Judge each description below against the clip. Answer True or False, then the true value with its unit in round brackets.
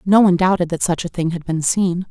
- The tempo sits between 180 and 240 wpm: False (285 wpm)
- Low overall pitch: False (175 Hz)